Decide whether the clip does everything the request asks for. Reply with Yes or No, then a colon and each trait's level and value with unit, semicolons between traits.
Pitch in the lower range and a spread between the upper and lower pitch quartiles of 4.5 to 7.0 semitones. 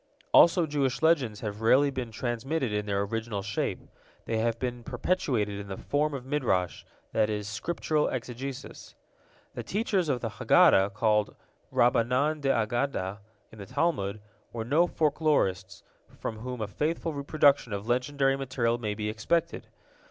Yes: low, 120 Hz; average, 5.2 semitones